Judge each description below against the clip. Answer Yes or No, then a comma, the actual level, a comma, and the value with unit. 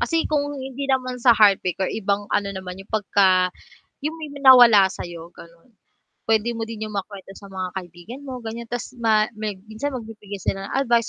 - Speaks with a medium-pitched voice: No, high, 215 Hz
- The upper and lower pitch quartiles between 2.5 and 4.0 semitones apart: No, average, 4.4 semitones